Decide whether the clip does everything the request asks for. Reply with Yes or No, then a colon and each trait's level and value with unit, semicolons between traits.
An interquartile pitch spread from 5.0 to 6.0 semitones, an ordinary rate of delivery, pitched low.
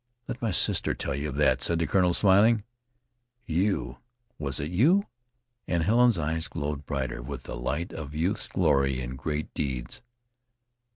Yes: wide, 5.5 semitones; average, 160 wpm; very low, 75 Hz